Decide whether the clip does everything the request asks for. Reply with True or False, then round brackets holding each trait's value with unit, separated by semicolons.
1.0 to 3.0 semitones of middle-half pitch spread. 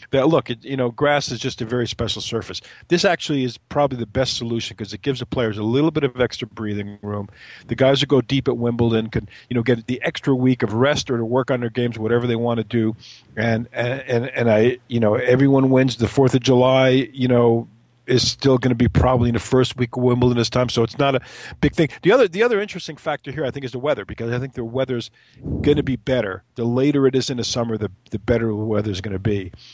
True (2.4 semitones)